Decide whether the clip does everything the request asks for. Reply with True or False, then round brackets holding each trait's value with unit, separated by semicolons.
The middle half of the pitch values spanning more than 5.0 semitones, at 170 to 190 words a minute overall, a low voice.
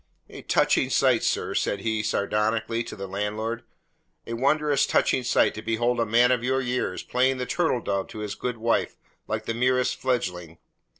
False (2.9 semitones; 180 wpm; 115 Hz)